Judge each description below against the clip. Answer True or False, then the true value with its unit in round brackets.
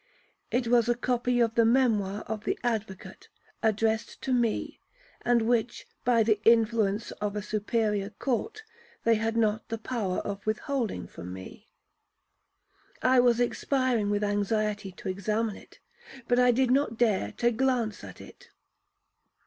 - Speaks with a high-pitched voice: True (225 Hz)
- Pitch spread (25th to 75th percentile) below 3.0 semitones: True (2.6 semitones)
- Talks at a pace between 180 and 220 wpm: False (150 wpm)